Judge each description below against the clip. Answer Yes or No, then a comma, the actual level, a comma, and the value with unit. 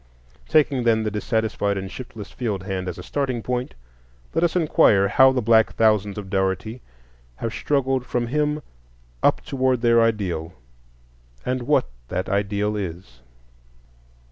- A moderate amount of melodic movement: Yes, average, 4.5 semitones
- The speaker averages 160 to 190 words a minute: No, average, 145 wpm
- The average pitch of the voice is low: Yes, low, 110 Hz